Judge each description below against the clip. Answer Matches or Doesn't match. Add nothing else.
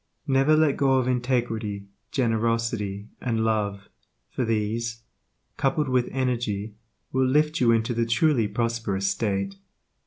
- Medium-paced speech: Doesn't match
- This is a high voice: Doesn't match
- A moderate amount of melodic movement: Matches